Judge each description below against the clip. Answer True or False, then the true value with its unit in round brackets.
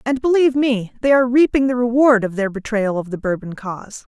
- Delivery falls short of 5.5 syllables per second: False (5.9 syllables/s)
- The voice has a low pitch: False (235 Hz)